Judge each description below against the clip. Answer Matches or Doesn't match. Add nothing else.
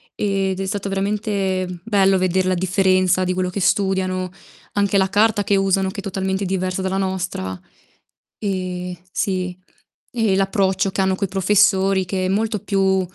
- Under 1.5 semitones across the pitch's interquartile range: Matches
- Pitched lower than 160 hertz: Doesn't match